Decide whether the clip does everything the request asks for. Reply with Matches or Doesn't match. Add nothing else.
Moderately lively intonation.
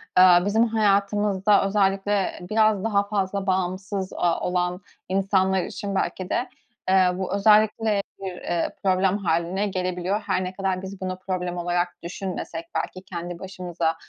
Doesn't match